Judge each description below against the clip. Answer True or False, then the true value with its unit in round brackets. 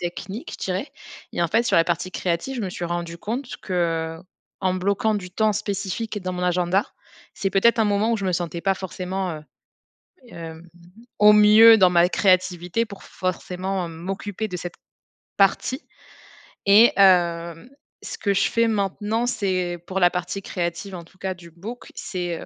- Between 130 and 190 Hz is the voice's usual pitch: True (185 Hz)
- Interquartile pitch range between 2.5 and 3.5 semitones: True (2.9 semitones)